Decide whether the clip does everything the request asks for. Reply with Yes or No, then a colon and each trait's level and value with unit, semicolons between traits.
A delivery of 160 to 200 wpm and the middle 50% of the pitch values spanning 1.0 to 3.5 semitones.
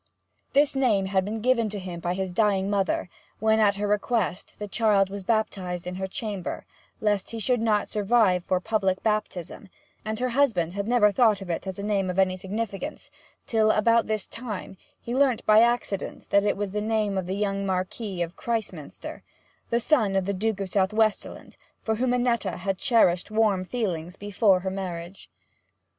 Yes: average, 180 wpm; average, 2.7 semitones